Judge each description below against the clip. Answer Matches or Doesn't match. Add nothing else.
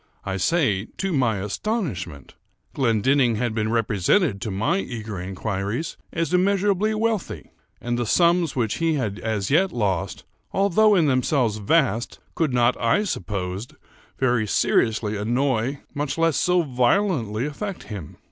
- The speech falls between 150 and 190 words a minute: Doesn't match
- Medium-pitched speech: Doesn't match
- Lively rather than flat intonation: Matches